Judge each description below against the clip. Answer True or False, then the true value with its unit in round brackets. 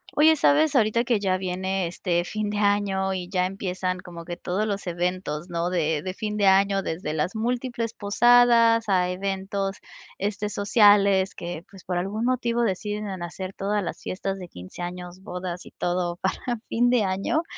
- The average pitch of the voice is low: False (195 Hz)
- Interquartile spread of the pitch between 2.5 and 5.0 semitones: True (2.9 semitones)